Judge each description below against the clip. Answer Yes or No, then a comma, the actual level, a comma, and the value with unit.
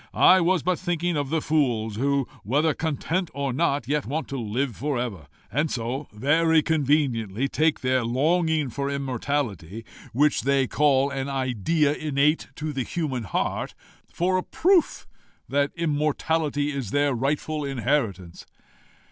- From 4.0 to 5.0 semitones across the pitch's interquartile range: No, average, 3.4 semitones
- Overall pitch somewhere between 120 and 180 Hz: Yes, medium, 140 Hz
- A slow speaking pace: No, average, 145 wpm